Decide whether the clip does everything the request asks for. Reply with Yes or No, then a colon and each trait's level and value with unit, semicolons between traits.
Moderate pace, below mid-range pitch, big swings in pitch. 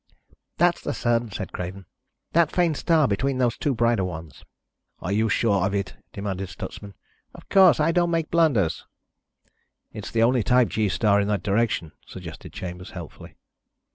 Yes: average, 165 wpm; low, 110 Hz; wide, 6.0 semitones